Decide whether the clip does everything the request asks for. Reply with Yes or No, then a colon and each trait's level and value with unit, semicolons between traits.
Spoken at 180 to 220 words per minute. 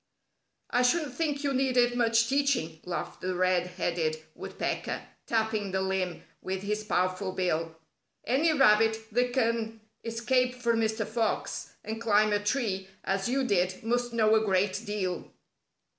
No: average, 145 wpm